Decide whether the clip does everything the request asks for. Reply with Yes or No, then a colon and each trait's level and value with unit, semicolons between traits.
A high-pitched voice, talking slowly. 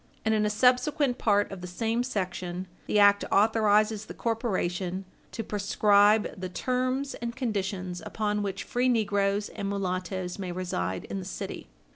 No: high, 205 Hz; average, 155 wpm